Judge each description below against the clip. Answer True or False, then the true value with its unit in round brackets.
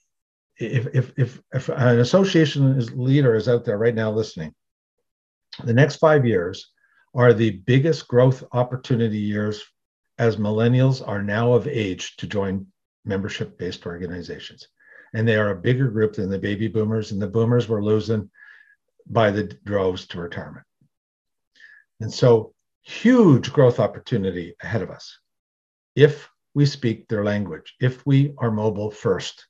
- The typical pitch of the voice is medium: False (115 Hz)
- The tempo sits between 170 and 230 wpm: False (150 wpm)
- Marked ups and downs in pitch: False (3.7 semitones)